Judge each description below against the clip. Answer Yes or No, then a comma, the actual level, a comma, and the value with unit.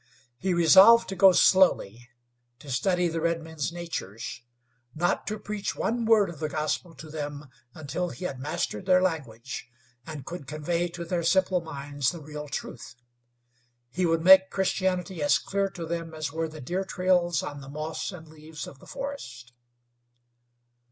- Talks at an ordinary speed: Yes, average, 165 wpm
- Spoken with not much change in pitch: No, average, 3.7 semitones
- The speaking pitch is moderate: Yes, medium, 165 Hz